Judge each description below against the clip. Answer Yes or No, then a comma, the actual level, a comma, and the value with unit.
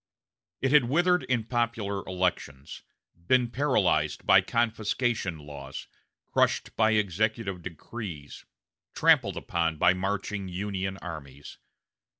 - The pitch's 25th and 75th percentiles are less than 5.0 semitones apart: No, average, 5.3 semitones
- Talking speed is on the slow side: Yes, slow, 105 wpm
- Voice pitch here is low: Yes, low, 100 Hz